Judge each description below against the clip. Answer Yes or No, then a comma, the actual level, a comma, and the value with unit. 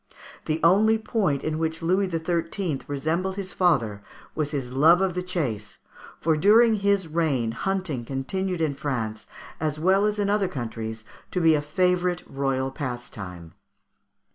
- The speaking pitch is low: No, medium, 160 Hz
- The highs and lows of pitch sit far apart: Yes, wide, 5.8 semitones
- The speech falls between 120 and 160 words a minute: Yes, average, 150 wpm